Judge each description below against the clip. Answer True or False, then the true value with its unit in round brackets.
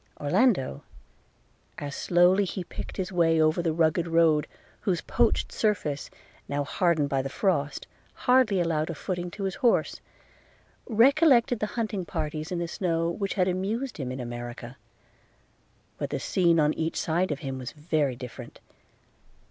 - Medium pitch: True (170 Hz)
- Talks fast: False (155 wpm)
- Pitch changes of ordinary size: True (4.3 semitones)